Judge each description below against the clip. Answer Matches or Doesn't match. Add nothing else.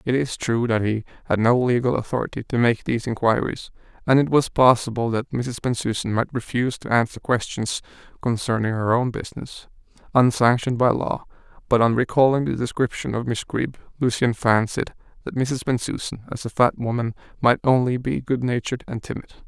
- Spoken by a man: Matches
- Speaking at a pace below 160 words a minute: Doesn't match